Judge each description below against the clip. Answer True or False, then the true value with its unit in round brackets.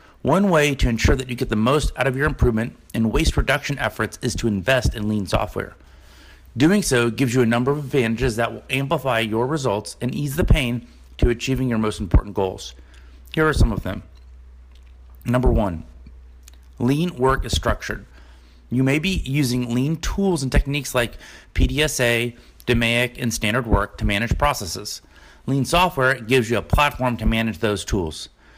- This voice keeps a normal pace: True (175 wpm)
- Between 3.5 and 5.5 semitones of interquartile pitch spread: True (5.1 semitones)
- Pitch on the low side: True (120 Hz)